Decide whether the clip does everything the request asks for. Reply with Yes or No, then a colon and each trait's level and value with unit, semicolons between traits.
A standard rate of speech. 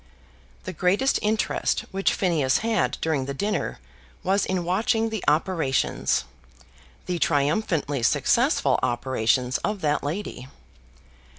No: slow, 110 wpm